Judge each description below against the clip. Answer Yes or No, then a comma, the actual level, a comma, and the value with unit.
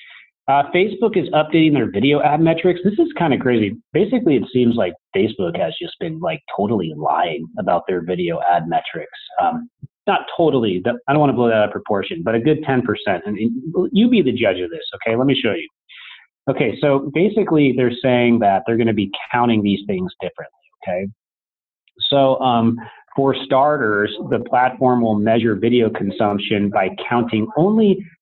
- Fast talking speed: No, average, 180 wpm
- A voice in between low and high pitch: No, low, 130 Hz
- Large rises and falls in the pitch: Yes, wide, 7.3 semitones